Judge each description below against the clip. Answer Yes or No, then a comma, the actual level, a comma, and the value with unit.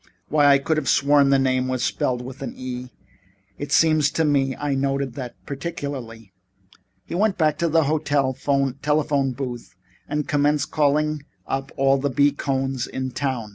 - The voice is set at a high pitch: No, medium, 140 Hz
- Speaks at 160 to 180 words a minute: Yes, average, 170 wpm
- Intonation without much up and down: Yes, narrow, 2.1 semitones